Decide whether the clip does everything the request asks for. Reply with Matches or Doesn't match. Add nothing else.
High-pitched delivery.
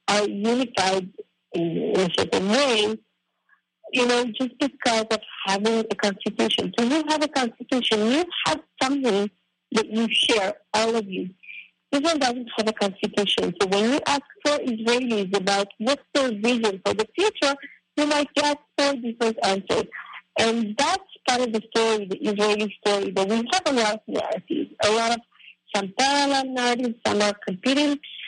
Matches